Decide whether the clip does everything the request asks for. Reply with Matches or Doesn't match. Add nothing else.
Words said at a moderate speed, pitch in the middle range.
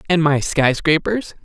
Matches